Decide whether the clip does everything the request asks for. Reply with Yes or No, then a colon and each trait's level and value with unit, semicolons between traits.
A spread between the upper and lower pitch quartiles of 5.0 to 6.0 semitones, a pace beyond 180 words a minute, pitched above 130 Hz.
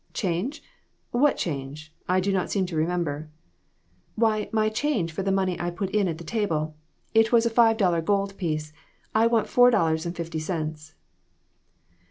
No: average, 5.3 semitones; average, 175 wpm; medium, 185 Hz